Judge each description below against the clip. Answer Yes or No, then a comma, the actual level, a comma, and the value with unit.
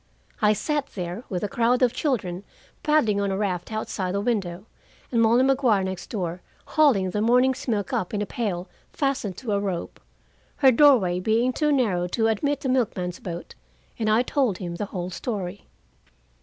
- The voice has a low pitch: No, high, 215 Hz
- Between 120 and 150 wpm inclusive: No, average, 180 wpm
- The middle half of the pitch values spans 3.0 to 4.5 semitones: No, average, 5.2 semitones